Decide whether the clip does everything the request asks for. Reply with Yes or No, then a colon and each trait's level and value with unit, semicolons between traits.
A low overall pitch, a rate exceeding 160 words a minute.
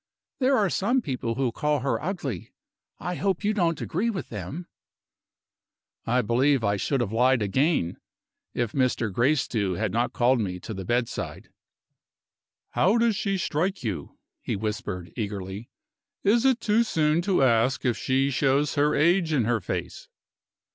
No: low, 130 Hz; average, 155 wpm